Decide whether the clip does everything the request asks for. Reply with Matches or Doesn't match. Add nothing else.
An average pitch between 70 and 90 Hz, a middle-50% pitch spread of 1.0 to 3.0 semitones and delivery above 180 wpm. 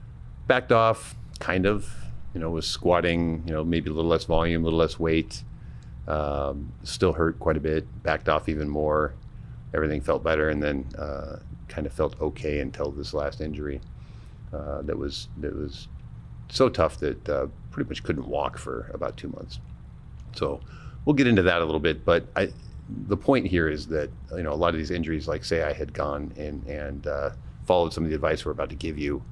Matches